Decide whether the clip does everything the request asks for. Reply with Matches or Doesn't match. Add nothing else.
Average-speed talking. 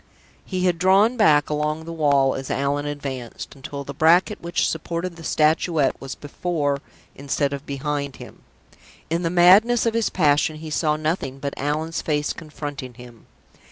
Matches